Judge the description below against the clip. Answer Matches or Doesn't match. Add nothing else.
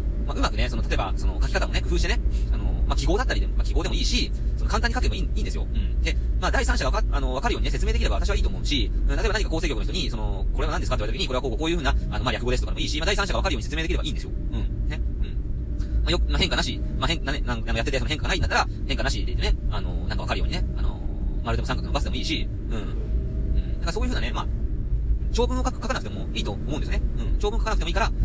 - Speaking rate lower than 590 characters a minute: Doesn't match